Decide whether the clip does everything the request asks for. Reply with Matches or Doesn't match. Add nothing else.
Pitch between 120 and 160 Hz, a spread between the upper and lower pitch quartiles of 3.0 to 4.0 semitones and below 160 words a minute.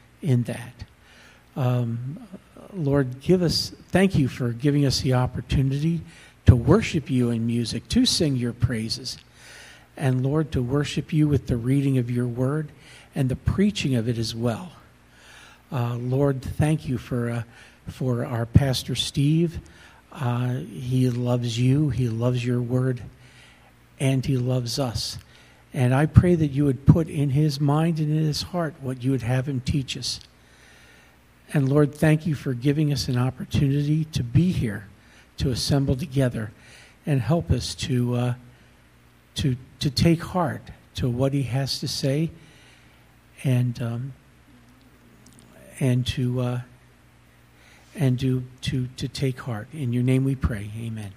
Matches